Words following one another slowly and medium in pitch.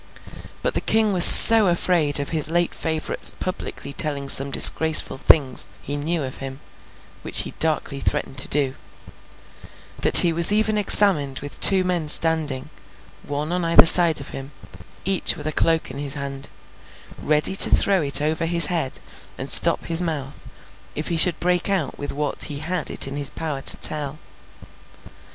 No: average, 170 wpm; medium, 155 Hz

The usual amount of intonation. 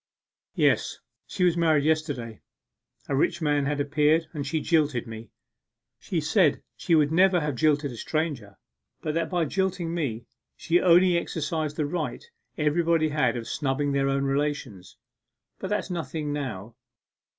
Yes: average, 3.2 semitones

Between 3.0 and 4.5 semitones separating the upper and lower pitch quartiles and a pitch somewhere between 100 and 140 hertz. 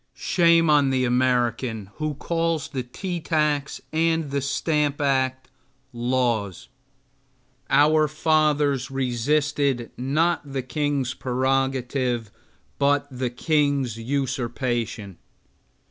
Yes: average, 3.3 semitones; low, 135 Hz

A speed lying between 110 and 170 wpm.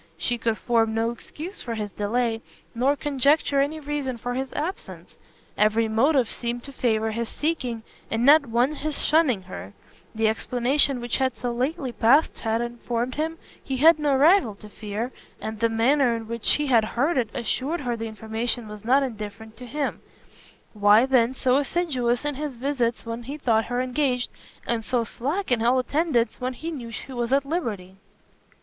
No: average, 180 wpm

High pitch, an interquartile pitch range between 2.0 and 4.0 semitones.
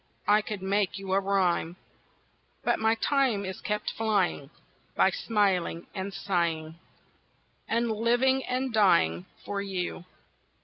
Yes: high, 200 Hz; average, 3.5 semitones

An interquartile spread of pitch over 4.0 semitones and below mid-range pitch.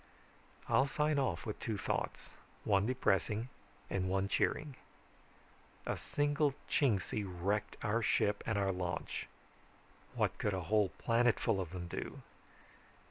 Yes: average, 4.6 semitones; low, 105 Hz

